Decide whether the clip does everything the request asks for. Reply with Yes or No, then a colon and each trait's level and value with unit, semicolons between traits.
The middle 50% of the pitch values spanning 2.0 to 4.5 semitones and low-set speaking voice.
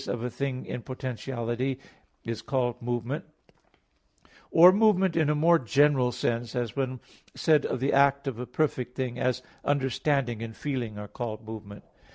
Yes: average, 2.9 semitones; low, 130 Hz